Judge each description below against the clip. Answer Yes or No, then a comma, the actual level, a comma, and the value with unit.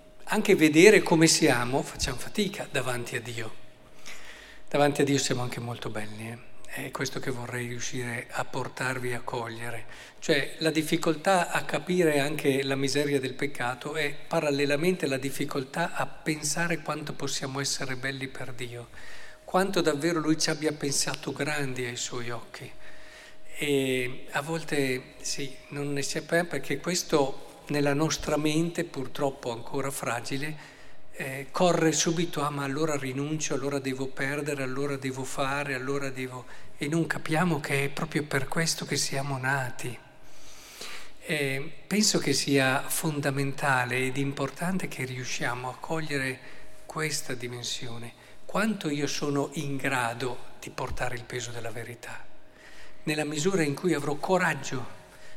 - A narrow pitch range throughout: No, average, 3.2 semitones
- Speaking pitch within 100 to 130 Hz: No, medium, 140 Hz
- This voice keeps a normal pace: Yes, average, 140 wpm